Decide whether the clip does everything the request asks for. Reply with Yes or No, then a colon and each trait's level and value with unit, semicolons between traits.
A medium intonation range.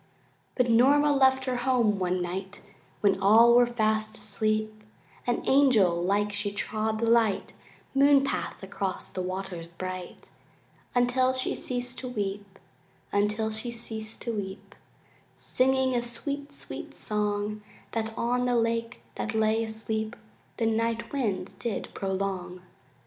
Yes: average, 3.3 semitones